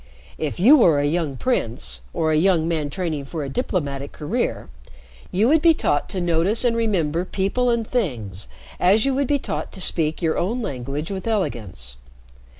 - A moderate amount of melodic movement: No, wide, 7.3 semitones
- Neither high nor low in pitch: Yes, medium, 170 Hz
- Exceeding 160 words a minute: Yes, average, 180 wpm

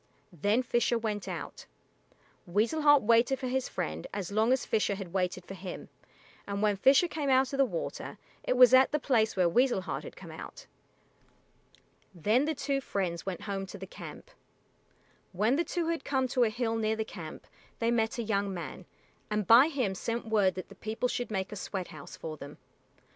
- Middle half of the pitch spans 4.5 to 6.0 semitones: Yes, average, 4.9 semitones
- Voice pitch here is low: No, high, 220 Hz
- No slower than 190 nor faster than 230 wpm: Yes, average, 200 wpm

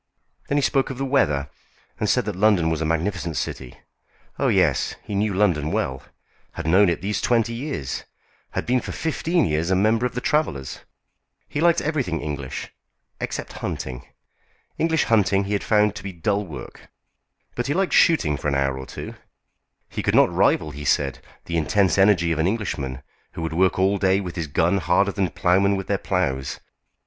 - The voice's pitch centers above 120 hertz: No, very low, 95 Hz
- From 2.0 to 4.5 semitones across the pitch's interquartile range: No, wide, 5.4 semitones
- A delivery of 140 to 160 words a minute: No, average, 190 wpm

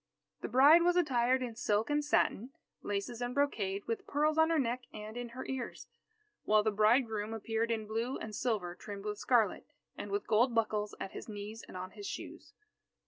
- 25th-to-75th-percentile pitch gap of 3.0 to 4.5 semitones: Yes, average, 3.5 semitones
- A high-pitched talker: Yes, high, 230 Hz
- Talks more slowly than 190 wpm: No, average, 195 wpm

